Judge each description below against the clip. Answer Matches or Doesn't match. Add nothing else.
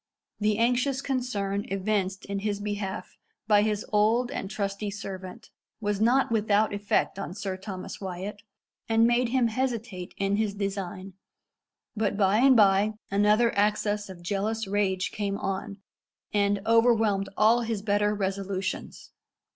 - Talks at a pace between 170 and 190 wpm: Doesn't match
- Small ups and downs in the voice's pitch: Matches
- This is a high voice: Matches